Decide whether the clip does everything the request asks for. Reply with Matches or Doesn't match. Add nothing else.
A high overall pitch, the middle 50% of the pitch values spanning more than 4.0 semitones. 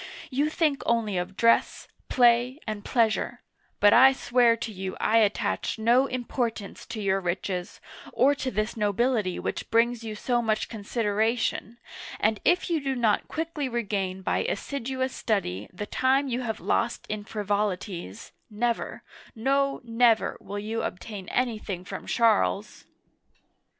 Doesn't match